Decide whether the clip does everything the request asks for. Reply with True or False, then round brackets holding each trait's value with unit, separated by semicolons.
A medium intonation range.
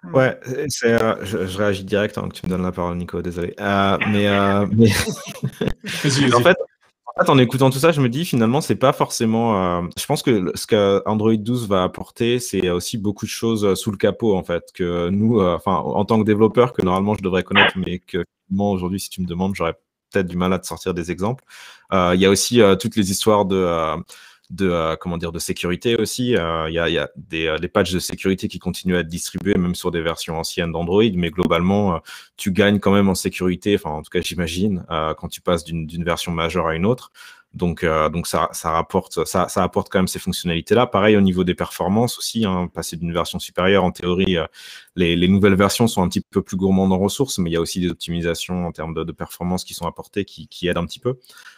True (3.1 semitones)